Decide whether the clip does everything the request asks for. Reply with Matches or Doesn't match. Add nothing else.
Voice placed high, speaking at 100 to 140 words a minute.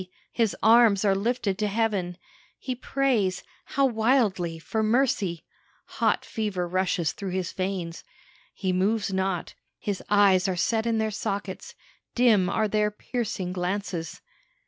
Matches